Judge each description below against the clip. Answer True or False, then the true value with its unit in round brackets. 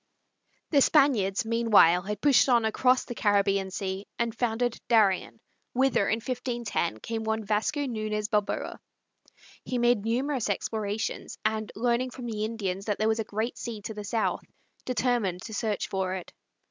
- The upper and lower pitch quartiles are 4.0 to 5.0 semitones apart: False (2.8 semitones)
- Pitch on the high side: True (220 Hz)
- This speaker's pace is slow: False (160 wpm)